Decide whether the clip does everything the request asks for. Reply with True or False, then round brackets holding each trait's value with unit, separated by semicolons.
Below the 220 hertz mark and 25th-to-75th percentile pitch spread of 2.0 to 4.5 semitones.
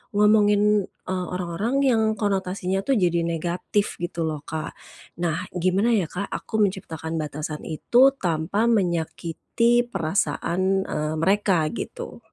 True (185 Hz; 3.9 semitones)